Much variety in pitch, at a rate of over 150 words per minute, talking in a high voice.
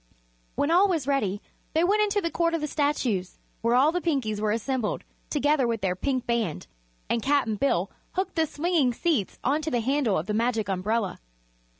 Yes: wide, 6.4 semitones; average, 190 wpm; very high, 265 Hz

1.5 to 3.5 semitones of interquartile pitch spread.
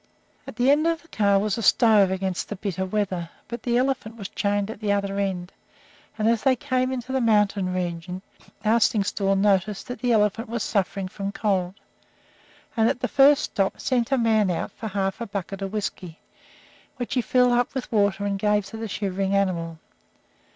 Yes: average, 3.2 semitones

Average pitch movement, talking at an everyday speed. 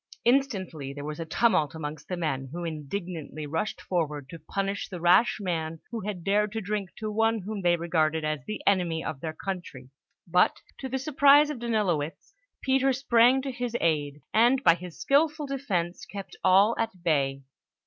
No: wide, 6.2 semitones; average, 180 wpm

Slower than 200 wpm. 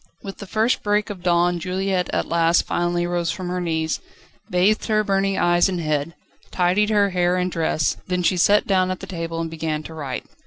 No: fast, 205 wpm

